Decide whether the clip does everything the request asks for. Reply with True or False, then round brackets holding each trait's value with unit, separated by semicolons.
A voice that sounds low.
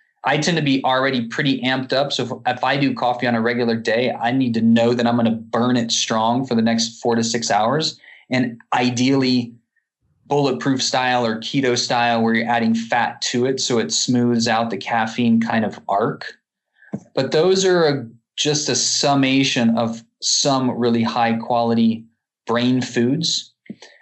True (120 Hz)